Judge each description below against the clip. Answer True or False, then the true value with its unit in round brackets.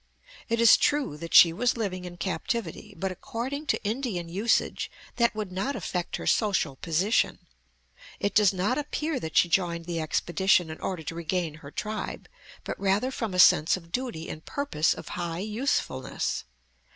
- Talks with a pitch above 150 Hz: True (190 Hz)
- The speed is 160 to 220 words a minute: True (170 wpm)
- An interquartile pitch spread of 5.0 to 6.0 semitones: True (5.5 semitones)